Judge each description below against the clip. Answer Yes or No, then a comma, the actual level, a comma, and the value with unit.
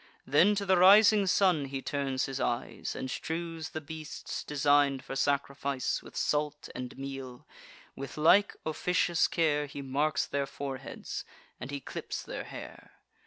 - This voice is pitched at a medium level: Yes, medium, 145 Hz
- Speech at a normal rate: Yes, average, 150 wpm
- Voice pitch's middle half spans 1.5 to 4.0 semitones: Yes, average, 3.1 semitones